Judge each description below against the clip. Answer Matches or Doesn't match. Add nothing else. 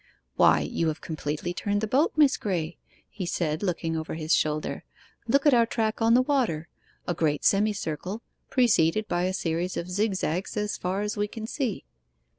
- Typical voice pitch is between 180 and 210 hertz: Matches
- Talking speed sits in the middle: Matches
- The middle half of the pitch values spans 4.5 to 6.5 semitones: Matches